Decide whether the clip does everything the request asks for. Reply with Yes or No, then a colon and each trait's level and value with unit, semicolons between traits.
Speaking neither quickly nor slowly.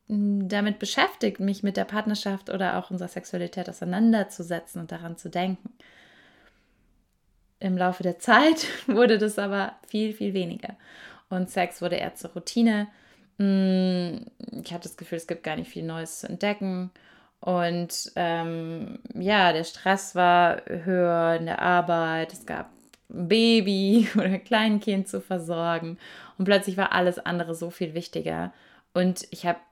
Yes: average, 145 wpm